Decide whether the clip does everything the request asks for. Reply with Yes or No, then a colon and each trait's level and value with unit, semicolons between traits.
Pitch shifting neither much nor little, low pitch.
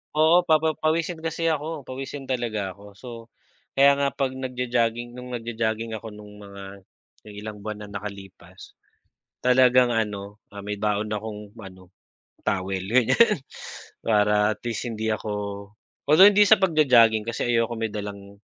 Yes: average, 4.0 semitones; low, 115 Hz